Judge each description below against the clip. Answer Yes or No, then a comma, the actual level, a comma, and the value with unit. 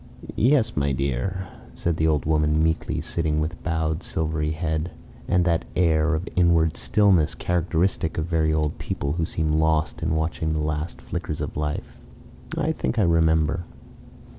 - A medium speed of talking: Yes, average, 160 wpm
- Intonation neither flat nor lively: No, narrow, 1.7 semitones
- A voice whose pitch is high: No, very low, 80 Hz